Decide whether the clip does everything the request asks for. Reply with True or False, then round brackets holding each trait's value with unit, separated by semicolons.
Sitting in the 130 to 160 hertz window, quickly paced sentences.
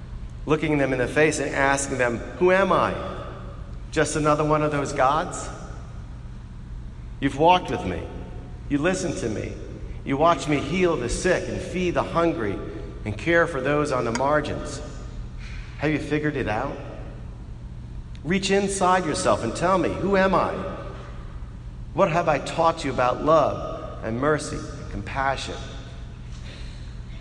False (135 Hz; 150 wpm)